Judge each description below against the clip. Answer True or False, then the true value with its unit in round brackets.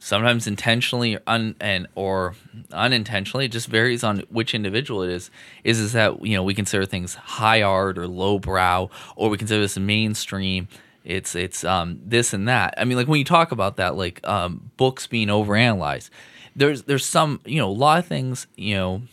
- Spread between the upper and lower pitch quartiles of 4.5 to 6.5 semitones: False (3.7 semitones)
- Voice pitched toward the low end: True (105 Hz)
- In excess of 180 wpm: True (200 wpm)